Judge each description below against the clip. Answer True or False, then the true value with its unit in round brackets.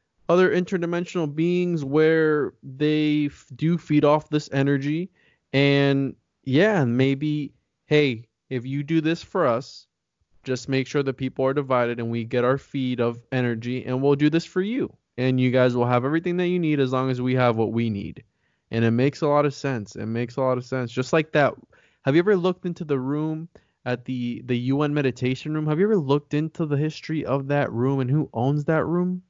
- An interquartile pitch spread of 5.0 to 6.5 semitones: False (3.6 semitones)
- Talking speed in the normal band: False (210 wpm)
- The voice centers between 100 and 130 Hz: False (140 Hz)